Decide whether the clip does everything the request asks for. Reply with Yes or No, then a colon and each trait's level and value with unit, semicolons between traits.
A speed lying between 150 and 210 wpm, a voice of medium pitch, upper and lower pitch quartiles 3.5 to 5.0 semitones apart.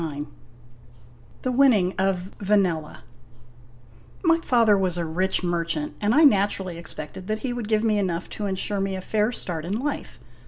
No: average, 165 wpm; high, 195 Hz; average, 3.8 semitones